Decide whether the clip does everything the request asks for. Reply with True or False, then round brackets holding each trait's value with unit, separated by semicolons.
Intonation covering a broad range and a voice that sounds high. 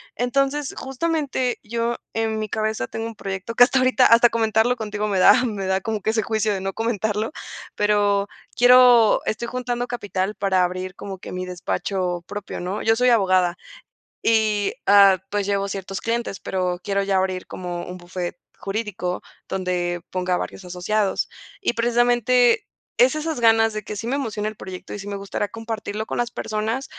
False (3.5 semitones; 215 Hz)